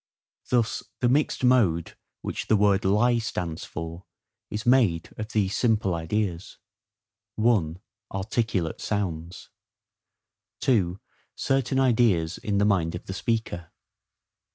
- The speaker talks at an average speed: No, slow, 110 wpm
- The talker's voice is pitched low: Yes, low, 100 Hz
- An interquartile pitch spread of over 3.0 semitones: Yes, average, 5.1 semitones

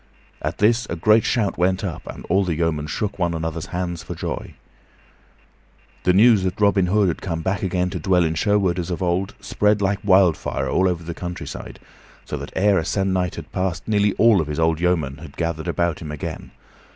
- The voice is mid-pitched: No, very low, 90 Hz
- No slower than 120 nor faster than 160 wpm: No, fast, 205 wpm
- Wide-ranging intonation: No, average, 3.0 semitones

